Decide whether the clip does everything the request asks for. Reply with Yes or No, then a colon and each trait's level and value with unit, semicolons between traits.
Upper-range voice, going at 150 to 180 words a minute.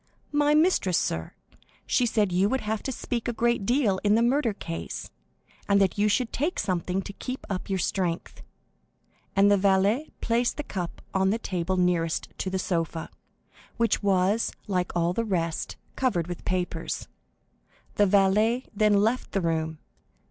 Yes: high, 200 Hz; average, 165 wpm